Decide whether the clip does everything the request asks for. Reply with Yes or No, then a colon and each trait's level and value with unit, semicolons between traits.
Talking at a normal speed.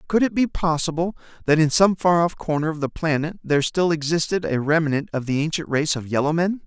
No: fast, 225 wpm